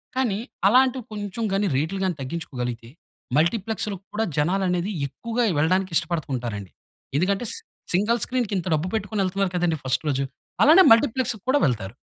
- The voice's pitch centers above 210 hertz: No, high, 190 Hz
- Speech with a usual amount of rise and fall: No, wide, 6.3 semitones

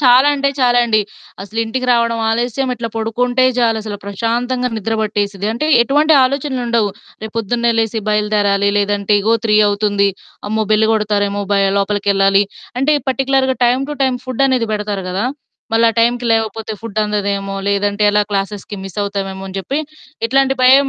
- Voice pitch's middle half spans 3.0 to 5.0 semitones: Yes, average, 3.4 semitones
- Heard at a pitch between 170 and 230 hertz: Yes, high, 220 Hz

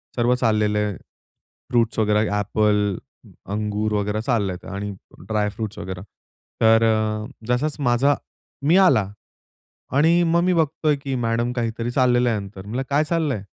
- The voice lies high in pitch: No, low, 115 Hz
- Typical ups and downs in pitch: Yes, average, 3.5 semitones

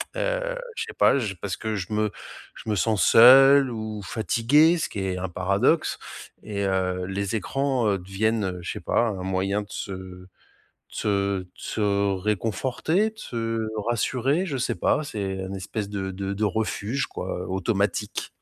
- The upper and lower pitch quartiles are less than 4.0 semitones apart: No, average, 4.3 semitones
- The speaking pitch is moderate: No, low, 105 Hz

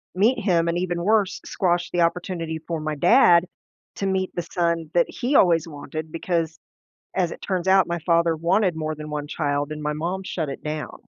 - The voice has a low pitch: No, medium, 170 Hz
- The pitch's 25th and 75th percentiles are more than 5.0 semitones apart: No, average, 2.8 semitones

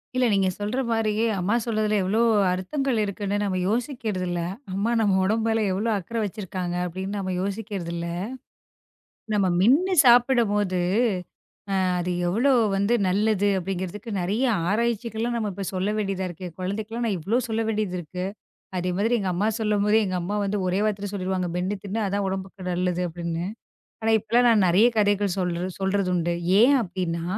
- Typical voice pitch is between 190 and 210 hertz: Yes, high, 200 Hz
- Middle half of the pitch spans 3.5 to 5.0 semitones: No, average, 3.1 semitones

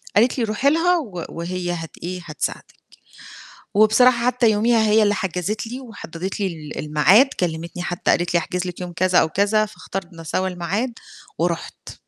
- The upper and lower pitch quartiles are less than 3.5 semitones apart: No, average, 4.2 semitones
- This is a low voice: No, medium, 185 Hz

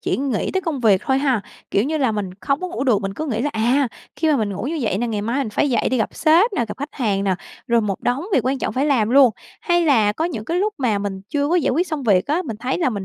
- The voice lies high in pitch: Yes, very high, 255 Hz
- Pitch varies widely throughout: Yes, wide, 5.7 semitones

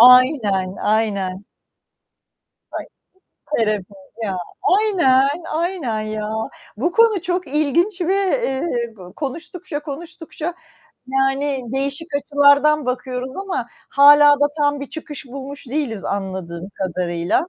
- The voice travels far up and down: Yes, wide, 6.4 semitones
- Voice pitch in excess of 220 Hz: Yes, very high, 275 Hz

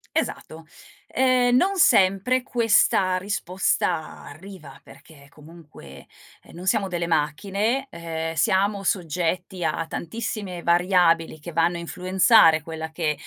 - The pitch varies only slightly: No, average, 3.6 semitones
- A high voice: No, medium, 175 Hz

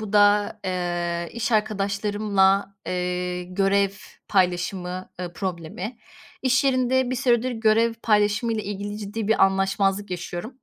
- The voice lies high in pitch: Yes, high, 200 Hz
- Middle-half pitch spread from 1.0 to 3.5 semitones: Yes, average, 3.0 semitones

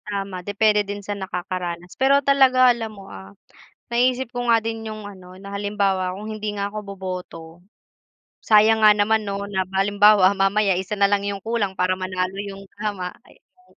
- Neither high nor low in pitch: No, high, 205 Hz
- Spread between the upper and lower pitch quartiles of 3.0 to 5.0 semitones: No, narrow, 2.4 semitones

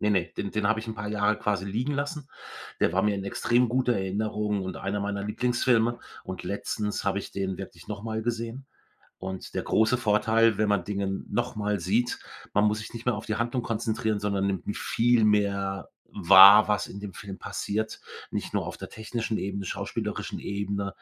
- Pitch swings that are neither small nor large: No, narrow, 2.2 semitones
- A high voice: No, low, 105 Hz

